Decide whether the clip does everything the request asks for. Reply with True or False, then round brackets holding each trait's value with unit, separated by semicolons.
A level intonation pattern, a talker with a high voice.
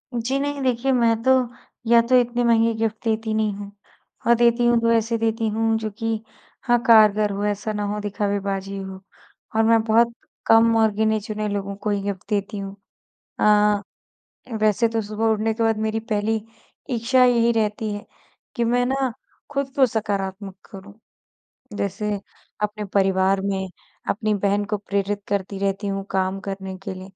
True (2.3 semitones; 215 Hz)